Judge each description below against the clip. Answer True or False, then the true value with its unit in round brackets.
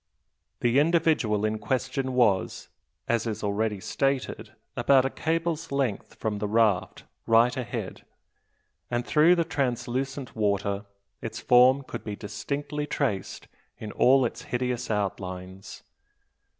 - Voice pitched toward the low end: True (120 Hz)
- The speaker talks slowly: True (125 wpm)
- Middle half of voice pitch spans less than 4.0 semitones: False (4.7 semitones)